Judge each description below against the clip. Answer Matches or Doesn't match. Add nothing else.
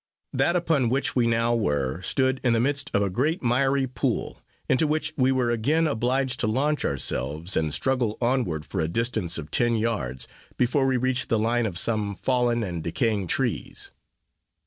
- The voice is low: Matches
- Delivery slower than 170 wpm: Doesn't match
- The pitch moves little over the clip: Doesn't match